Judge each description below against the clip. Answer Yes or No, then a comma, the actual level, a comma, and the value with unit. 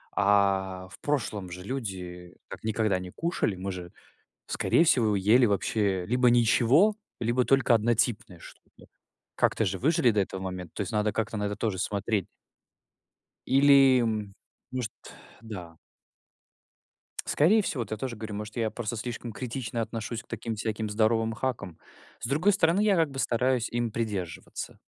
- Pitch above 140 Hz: No, low, 110 Hz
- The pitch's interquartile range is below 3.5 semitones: No, average, 3.8 semitones